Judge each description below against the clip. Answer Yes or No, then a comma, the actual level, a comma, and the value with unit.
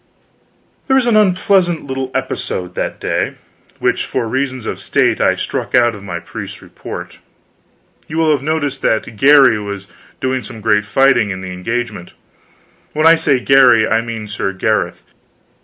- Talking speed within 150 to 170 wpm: Yes, average, 160 wpm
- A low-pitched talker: Yes, low, 120 Hz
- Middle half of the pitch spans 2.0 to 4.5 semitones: No, wide, 5.5 semitones